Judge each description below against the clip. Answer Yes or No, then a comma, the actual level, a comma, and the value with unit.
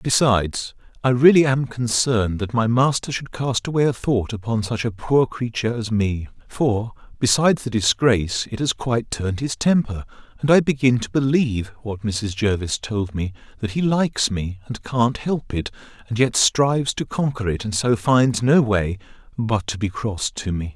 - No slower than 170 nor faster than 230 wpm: Yes, average, 190 wpm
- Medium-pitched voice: No, low, 115 Hz